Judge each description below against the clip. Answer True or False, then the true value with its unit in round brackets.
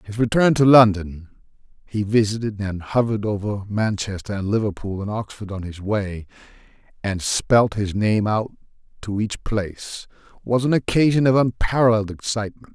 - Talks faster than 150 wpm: False (135 wpm)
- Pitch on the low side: True (105 Hz)